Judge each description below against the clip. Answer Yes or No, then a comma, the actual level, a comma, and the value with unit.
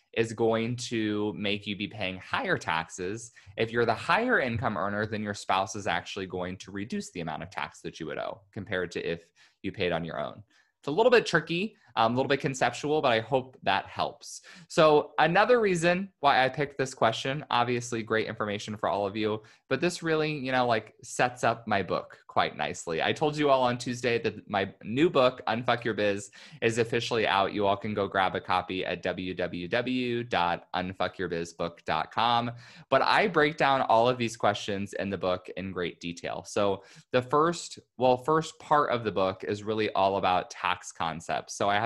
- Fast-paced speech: No, average, 195 wpm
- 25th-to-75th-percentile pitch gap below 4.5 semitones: No, average, 4.9 semitones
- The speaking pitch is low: Yes, low, 115 Hz